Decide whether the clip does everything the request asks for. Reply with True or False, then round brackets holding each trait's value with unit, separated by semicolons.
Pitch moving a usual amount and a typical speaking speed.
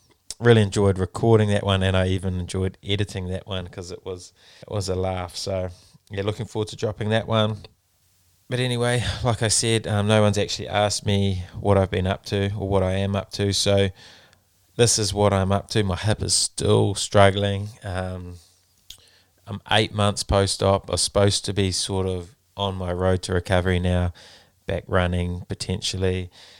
False (2.2 semitones; 185 wpm)